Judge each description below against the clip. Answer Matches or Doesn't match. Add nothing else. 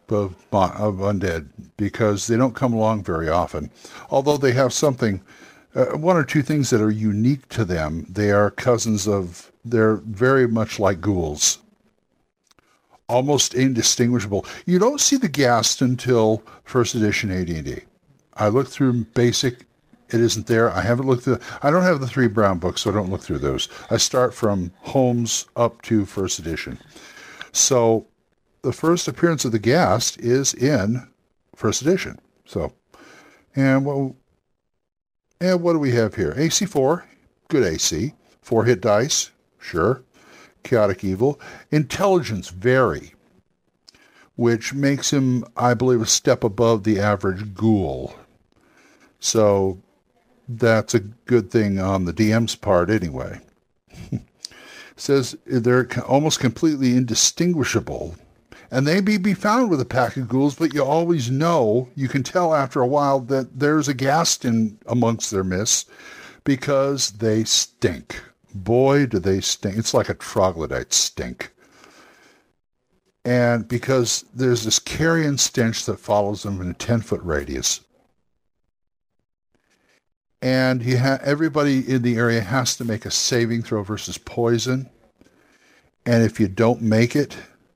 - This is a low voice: Matches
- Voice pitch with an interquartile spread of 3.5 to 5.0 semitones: Matches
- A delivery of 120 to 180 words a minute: Matches